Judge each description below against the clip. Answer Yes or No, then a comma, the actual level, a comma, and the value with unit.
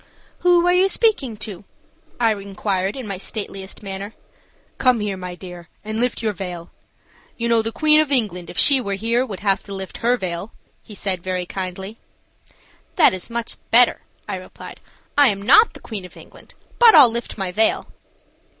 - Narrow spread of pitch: No, average, 4.2 semitones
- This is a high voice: Yes, high, 210 Hz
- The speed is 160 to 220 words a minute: Yes, average, 185 wpm